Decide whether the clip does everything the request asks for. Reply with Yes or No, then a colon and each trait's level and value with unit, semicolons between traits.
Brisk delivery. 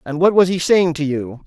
Yes: fast, 285 wpm